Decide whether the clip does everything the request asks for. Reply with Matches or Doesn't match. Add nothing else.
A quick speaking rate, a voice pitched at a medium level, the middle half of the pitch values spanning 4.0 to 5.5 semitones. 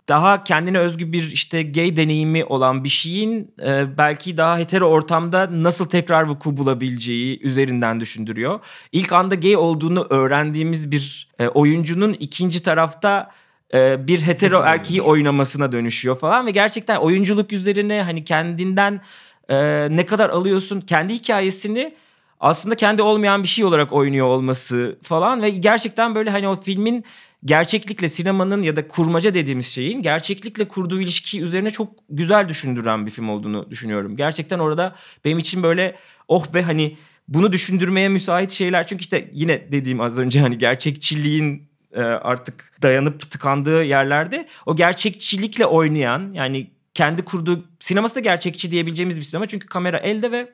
Matches